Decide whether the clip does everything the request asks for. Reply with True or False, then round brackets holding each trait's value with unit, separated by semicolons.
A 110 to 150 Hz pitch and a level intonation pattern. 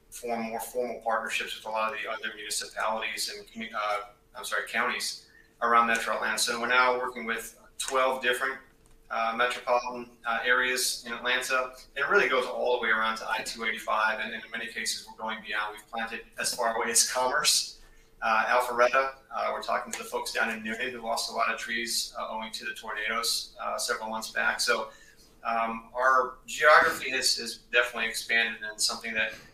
True (115 Hz; 2.0 semitones)